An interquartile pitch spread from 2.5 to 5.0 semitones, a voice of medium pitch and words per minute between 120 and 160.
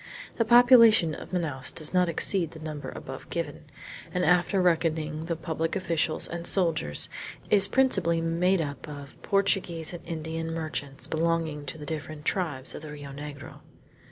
Yes: average, 2.8 semitones; medium, 165 Hz; average, 155 wpm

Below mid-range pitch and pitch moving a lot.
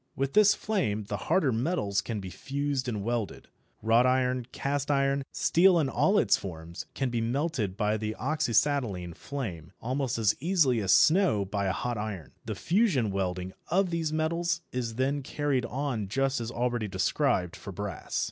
Yes: low, 125 Hz; wide, 5.8 semitones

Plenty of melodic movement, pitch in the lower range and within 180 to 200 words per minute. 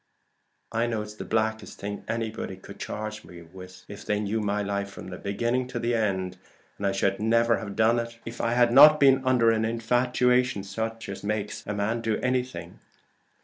No: narrow, 2.6 semitones; low, 110 Hz; average, 190 wpm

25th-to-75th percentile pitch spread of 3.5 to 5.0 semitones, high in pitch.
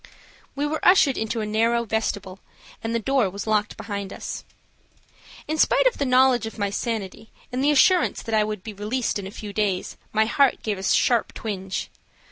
Yes: average, 3.8 semitones; high, 220 Hz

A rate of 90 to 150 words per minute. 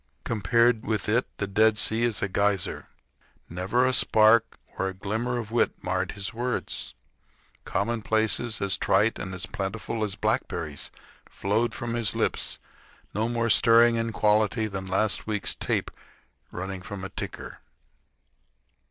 Yes: average, 145 wpm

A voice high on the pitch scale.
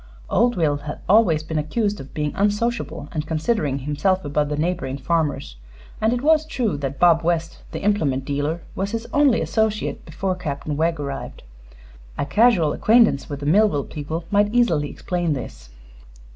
No: medium, 165 Hz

